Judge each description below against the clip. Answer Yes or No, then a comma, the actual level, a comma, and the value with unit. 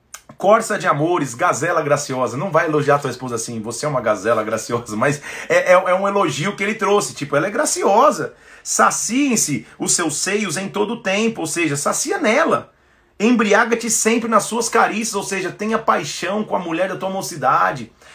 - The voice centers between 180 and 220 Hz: Yes, high, 190 Hz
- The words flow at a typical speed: No, fast, 190 wpm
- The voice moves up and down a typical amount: No, wide, 6.5 semitones